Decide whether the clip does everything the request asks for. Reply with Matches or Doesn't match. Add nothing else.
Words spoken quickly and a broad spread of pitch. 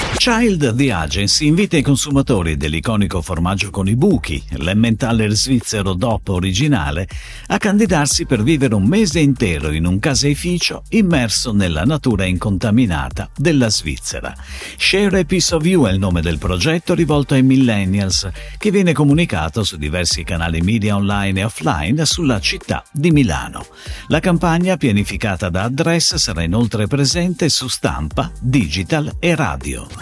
Doesn't match